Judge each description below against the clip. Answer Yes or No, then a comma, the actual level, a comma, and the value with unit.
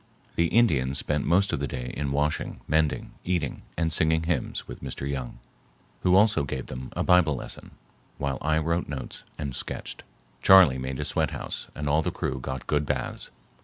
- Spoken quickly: No, average, 180 wpm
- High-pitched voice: No, very low, 75 Hz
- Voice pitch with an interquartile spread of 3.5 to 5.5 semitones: Yes, average, 3.8 semitones